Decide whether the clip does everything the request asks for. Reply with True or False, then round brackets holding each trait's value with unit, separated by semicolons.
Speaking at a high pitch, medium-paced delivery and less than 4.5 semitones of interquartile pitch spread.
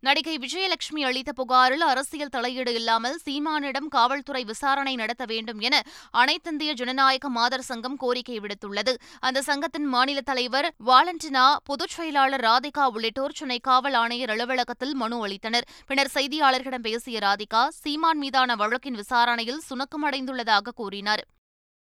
True (260 Hz; 120 wpm; 2.9 semitones)